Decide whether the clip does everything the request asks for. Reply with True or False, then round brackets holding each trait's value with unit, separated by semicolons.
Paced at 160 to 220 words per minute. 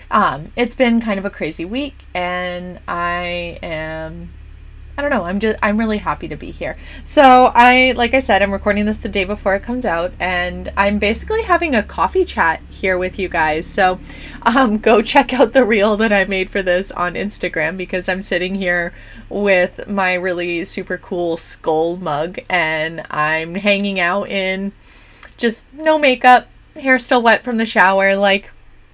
True (180 wpm)